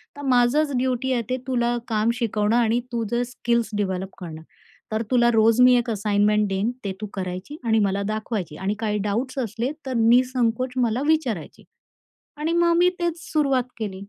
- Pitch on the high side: Yes, high, 235 Hz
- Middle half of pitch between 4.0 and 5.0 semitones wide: No, average, 3.3 semitones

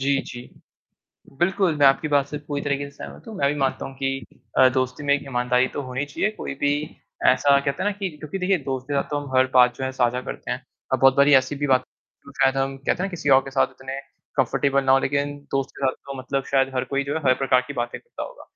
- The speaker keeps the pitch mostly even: Yes, narrow, 1.6 semitones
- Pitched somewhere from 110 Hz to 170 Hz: Yes, low, 135 Hz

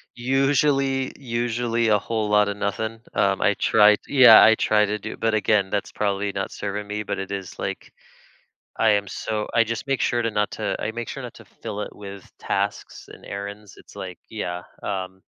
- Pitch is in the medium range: No, low, 105 Hz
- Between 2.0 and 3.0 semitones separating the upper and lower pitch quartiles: Yes, narrow, 2.4 semitones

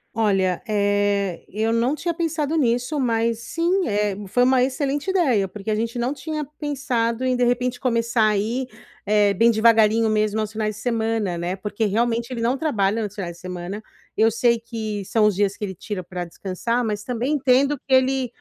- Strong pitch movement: No, average, 3.5 semitones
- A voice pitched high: Yes, high, 230 Hz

